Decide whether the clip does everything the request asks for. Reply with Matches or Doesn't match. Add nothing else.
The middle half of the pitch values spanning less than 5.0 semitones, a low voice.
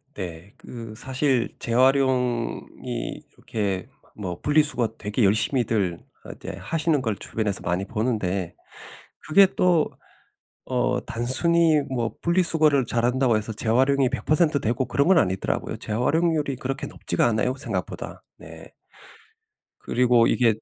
Matches